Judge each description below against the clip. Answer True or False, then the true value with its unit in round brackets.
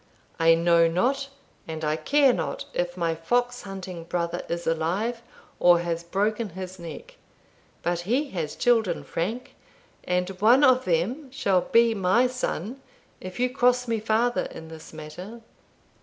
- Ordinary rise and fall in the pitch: False (6.2 semitones)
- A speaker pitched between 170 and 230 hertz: True (190 Hz)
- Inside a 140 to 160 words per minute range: True (150 wpm)